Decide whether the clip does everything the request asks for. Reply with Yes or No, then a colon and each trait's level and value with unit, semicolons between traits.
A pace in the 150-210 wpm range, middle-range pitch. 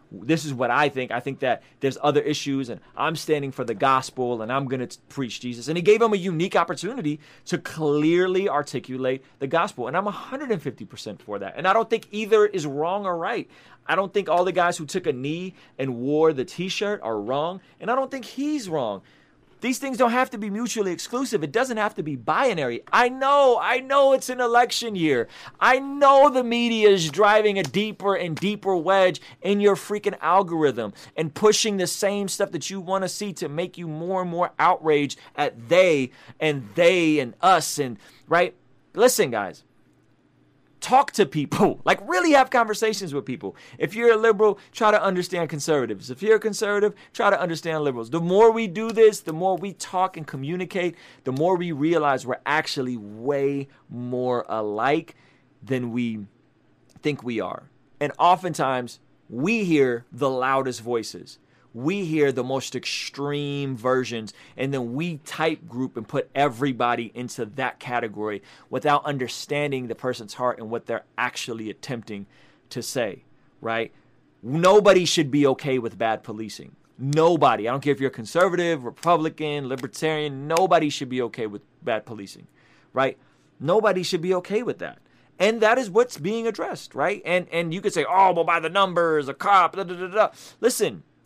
Yes: average, 180 wpm; medium, 160 Hz